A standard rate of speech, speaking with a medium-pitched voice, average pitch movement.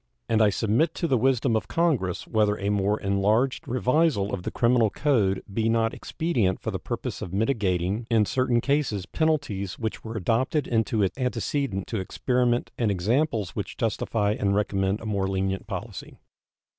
No: average, 170 wpm; low, 110 Hz; average, 4.1 semitones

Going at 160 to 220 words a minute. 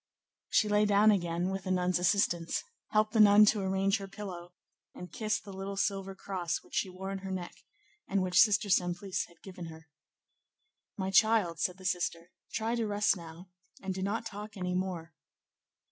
Yes: average, 185 wpm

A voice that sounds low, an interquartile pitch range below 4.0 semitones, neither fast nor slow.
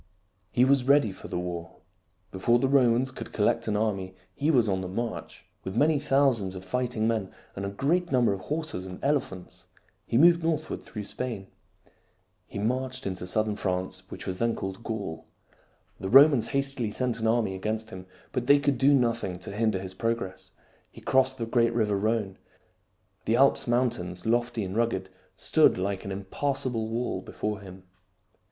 No: low, 110 Hz; average, 5.1 semitones; average, 175 wpm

